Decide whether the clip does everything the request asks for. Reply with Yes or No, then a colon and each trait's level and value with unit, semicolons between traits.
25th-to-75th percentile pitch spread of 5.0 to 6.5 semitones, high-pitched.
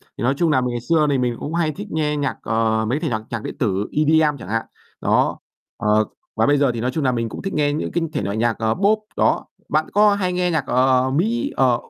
No: average, 5.3 semitones; low, 135 Hz